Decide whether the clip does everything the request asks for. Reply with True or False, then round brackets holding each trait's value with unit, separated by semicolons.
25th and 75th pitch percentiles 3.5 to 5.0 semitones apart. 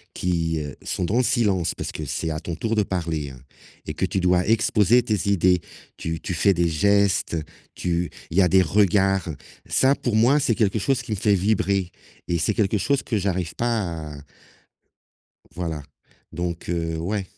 True (4.0 semitones)